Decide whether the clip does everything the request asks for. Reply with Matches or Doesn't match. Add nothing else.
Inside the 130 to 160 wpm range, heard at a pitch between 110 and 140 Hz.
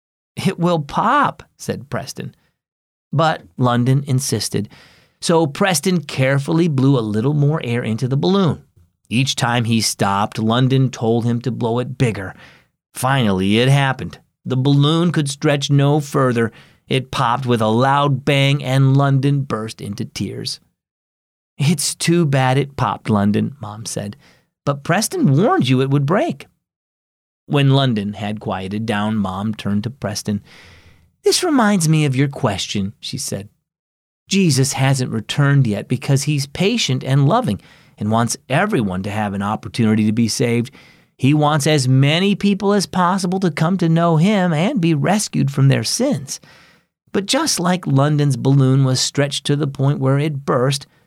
Matches